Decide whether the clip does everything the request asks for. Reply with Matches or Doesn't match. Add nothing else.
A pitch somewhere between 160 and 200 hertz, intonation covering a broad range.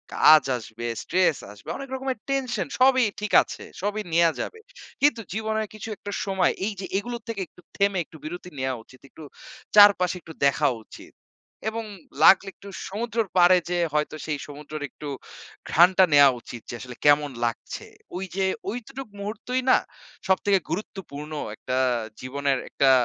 Matches